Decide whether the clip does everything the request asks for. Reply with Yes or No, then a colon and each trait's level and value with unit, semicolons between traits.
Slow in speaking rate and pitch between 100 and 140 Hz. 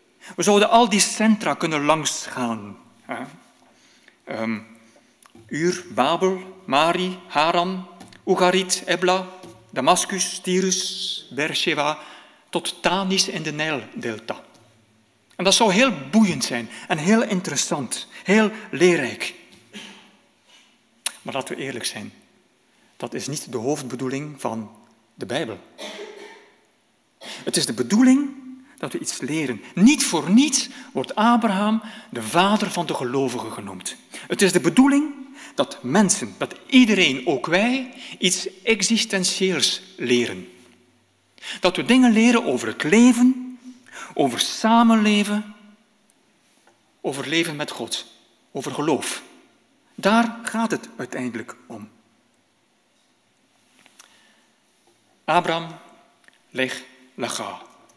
No: slow, 105 wpm; medium, 185 Hz